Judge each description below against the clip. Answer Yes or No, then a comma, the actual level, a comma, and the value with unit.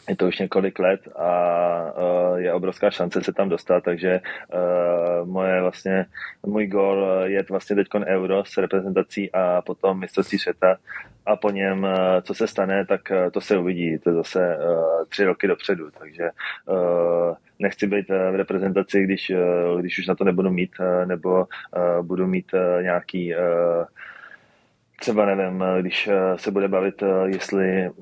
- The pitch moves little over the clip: Yes, narrow, 1.4 semitones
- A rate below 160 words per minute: Yes, average, 140 wpm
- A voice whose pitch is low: Yes, very low, 95 Hz